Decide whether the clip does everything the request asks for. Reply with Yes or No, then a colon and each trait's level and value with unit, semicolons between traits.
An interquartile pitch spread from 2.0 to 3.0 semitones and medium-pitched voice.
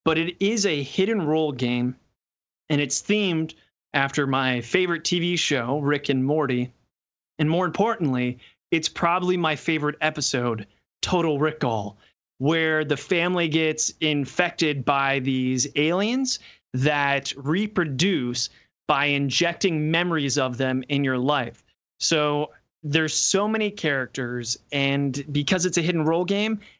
No: average, 4.2 semitones; medium, 150 Hz